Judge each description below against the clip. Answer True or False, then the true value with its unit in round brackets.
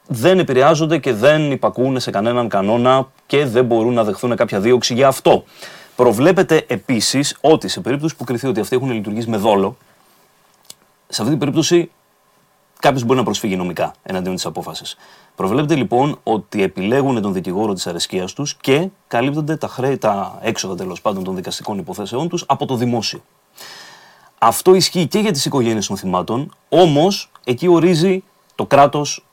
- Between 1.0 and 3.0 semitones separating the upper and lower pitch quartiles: False (5.5 semitones)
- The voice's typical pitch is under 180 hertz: True (135 Hz)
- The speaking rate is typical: True (160 wpm)